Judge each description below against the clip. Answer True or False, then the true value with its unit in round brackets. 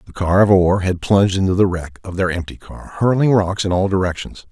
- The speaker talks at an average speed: False (240 wpm)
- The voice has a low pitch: True (95 Hz)